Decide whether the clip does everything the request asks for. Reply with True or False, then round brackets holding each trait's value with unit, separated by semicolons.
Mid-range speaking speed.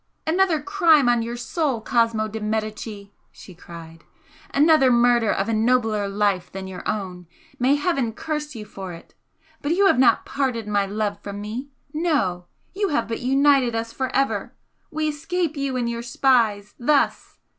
True (165 wpm)